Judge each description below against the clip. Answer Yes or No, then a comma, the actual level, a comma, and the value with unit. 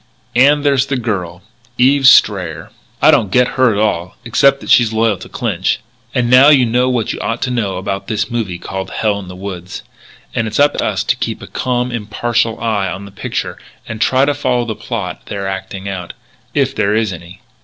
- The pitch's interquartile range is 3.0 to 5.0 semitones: Yes, average, 4.5 semitones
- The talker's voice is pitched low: Yes, low, 110 Hz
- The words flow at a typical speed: No, fast, 210 wpm